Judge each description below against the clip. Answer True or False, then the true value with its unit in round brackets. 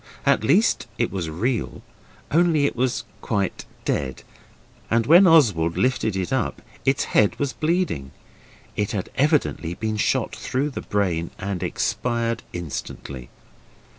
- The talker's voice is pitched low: True (115 Hz)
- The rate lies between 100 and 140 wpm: True (135 wpm)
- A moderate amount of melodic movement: False (7.2 semitones)